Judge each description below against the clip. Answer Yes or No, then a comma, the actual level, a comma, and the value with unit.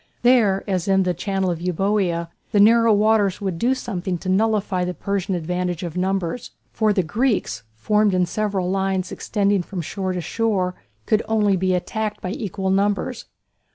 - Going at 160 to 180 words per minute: Yes, average, 170 wpm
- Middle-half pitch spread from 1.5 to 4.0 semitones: Yes, average, 2.7 semitones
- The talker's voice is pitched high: Yes, high, 195 Hz